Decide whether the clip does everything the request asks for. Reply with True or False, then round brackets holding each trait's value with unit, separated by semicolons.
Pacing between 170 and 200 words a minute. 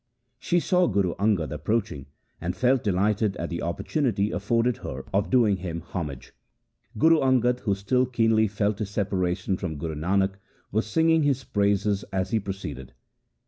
False (155 wpm)